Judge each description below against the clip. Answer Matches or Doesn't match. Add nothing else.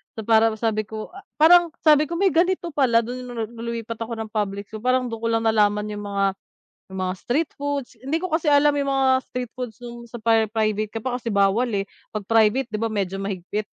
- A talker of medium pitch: Doesn't match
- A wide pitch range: Doesn't match